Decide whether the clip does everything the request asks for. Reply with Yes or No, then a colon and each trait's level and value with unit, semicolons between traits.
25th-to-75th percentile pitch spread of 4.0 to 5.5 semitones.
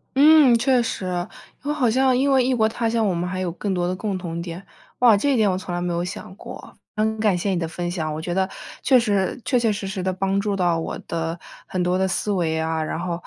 Yes: average, 4.4 semitones